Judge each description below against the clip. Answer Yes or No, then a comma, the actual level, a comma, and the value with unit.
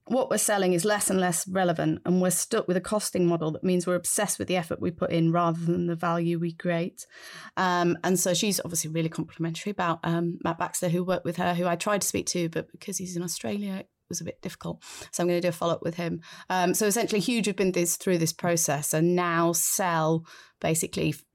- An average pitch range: No, narrow, 1.6 semitones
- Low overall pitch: No, medium, 175 Hz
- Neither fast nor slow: No, fast, 240 wpm